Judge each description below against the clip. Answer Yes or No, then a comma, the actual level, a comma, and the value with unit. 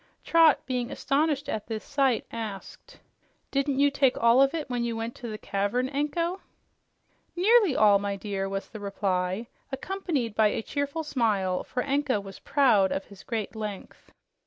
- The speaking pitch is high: Yes, high, 240 Hz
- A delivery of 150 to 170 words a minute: Yes, average, 165 wpm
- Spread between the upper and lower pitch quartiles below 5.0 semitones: No, wide, 5.6 semitones